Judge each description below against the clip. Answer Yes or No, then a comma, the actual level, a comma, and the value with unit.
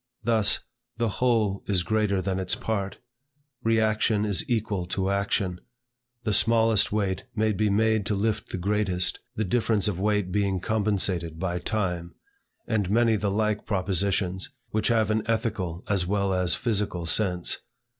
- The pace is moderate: Yes, average, 150 wpm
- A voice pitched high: No, low, 100 Hz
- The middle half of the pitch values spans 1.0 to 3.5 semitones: Yes, average, 2.7 semitones